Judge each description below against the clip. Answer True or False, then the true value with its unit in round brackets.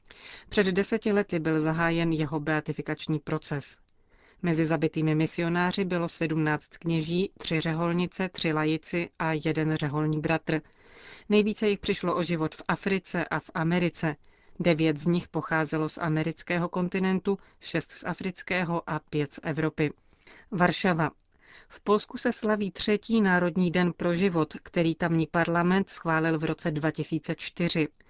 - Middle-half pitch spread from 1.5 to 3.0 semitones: True (2.4 semitones)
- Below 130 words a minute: False (135 wpm)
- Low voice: False (170 Hz)